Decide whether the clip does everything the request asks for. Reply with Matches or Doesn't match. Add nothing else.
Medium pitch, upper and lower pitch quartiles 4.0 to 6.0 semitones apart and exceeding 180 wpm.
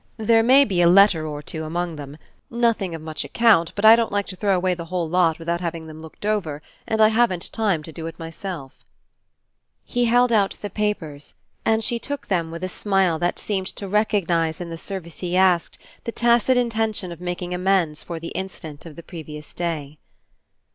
Matches